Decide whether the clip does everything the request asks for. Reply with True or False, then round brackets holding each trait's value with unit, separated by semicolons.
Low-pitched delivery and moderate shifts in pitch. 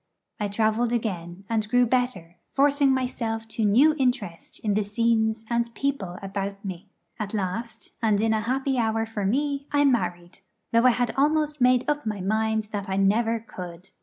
False (225 Hz; 3.6 semitones)